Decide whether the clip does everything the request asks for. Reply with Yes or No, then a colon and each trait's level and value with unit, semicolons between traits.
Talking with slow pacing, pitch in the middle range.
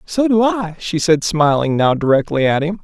No: fast, 210 wpm; medium, 170 Hz